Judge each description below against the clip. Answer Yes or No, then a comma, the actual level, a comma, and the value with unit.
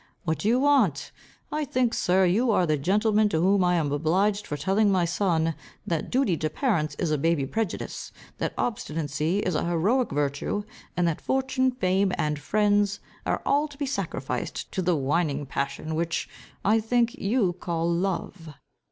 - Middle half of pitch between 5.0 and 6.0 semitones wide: Yes, average, 5.3 semitones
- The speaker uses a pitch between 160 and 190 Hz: Yes, medium, 185 Hz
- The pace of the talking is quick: No, average, 175 wpm